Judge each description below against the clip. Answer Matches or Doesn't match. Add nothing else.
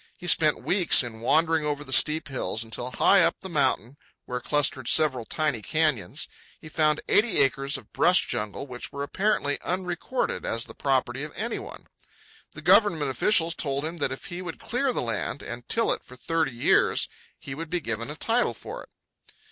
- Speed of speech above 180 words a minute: Matches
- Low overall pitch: Doesn't match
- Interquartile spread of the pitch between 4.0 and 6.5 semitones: Matches